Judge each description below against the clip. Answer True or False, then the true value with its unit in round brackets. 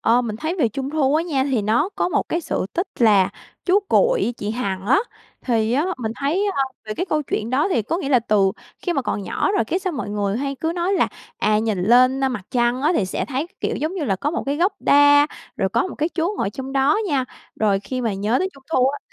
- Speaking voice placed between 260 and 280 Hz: True (265 Hz)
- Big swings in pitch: True (6.1 semitones)